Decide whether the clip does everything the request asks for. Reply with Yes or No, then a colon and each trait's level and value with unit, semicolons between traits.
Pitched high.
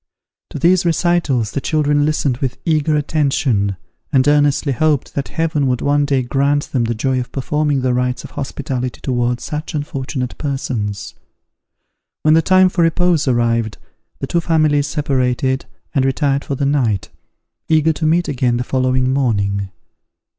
No: medium, 140 Hz